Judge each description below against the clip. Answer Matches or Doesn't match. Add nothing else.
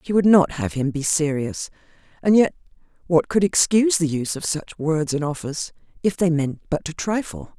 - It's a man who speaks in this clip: Doesn't match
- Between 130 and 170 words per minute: Doesn't match